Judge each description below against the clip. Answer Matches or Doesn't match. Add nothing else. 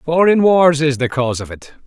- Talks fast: Matches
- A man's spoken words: Matches